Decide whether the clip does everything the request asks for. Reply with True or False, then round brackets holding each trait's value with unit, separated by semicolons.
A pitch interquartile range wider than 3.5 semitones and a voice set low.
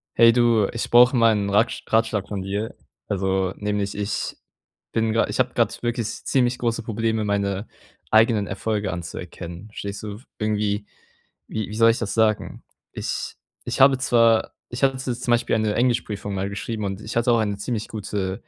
False (2.4 semitones; 110 Hz)